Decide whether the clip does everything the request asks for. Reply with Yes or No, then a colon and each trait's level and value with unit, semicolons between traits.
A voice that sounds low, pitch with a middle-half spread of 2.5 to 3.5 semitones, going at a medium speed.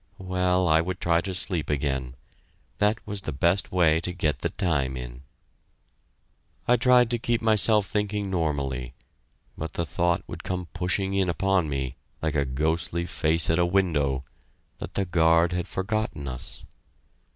No: very low, 85 Hz; average, 4.2 semitones; average, 160 wpm